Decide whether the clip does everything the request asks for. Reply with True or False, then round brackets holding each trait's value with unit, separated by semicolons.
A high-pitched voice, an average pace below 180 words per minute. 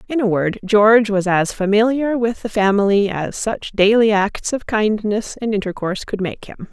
False (210 Hz; 190 wpm)